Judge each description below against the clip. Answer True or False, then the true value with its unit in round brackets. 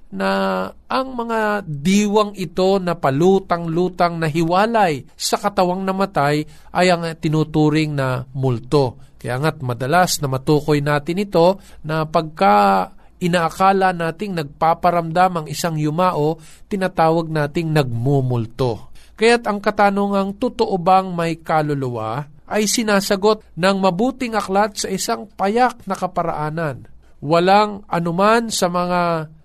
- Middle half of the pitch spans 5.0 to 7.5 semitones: False (4.6 semitones)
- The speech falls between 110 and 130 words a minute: True (115 wpm)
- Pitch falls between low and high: True (175 Hz)